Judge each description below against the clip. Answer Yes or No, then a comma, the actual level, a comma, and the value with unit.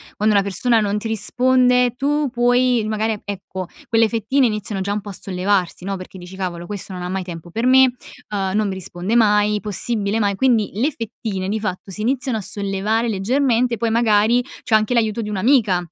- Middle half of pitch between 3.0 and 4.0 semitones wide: Yes, average, 3.5 semitones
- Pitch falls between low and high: No, high, 215 Hz